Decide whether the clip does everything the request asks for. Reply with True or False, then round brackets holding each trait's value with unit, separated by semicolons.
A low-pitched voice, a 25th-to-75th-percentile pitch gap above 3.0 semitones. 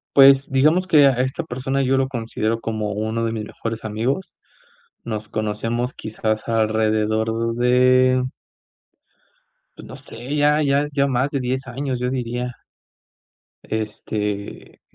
True (125 Hz; 3.4 semitones)